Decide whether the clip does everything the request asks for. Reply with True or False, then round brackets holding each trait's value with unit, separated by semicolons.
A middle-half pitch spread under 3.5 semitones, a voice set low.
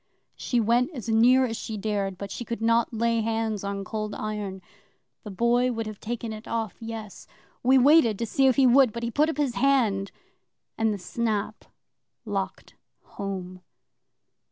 False (2.5 semitones; 225 Hz)